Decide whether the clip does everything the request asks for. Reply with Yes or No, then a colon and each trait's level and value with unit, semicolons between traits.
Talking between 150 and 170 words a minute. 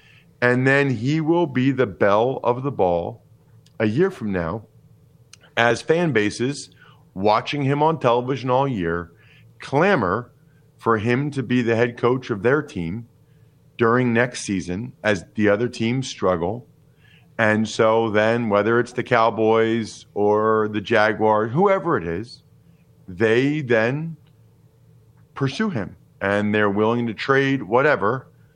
No: slow, 135 wpm